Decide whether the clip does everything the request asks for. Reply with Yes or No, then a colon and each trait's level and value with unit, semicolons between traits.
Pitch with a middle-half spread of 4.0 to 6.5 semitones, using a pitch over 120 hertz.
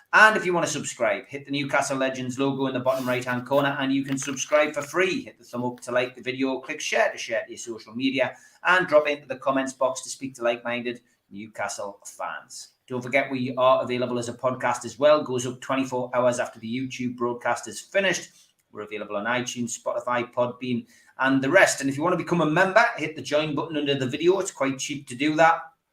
No: average, 3.4 semitones; low, 135 Hz